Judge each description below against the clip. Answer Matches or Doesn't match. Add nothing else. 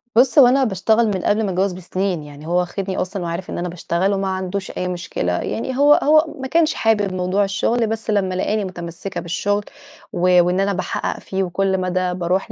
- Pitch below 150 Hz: Doesn't match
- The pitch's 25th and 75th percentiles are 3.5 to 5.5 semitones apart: Doesn't match